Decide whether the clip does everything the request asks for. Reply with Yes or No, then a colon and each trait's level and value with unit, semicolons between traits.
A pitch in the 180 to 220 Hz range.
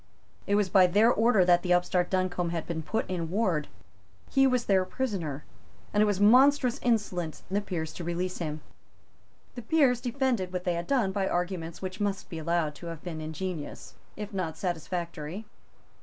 Yes: medium, 185 Hz